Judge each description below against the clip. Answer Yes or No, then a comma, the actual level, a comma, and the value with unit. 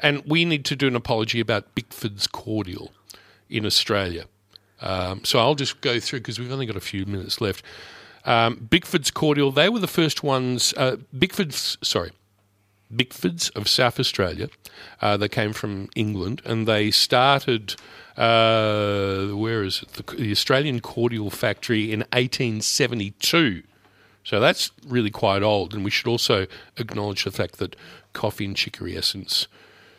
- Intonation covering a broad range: No, average, 4.0 semitones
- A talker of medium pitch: No, low, 115 Hz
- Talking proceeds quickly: No, average, 155 wpm